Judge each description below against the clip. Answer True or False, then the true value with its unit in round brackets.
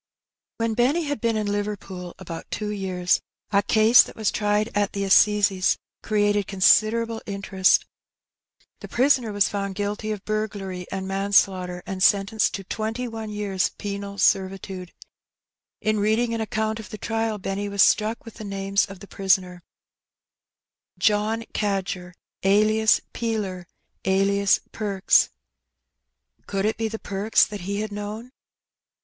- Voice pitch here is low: False (205 Hz)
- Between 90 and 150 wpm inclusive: True (140 wpm)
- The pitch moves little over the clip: True (2.0 semitones)